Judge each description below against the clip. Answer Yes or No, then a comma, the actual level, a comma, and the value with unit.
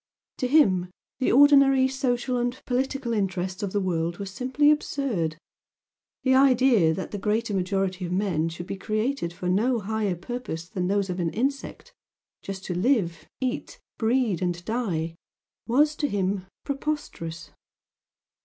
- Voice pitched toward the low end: No, high, 210 Hz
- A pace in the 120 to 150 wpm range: Yes, average, 145 wpm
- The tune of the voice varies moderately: No, wide, 6.2 semitones